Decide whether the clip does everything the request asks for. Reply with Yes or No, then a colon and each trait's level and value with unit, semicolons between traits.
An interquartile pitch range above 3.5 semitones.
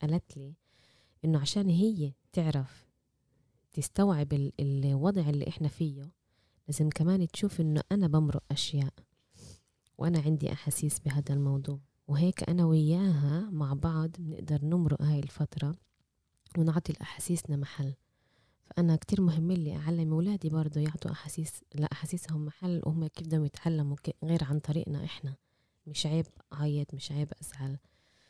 No: narrow, 2.5 semitones